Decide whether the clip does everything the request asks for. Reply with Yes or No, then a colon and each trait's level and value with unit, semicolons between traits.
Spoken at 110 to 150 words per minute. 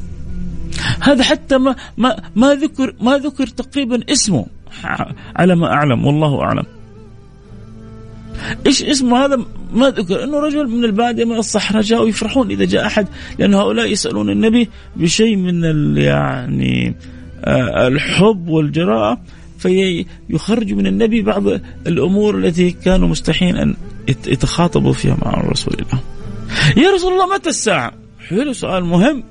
Yes: average, 130 wpm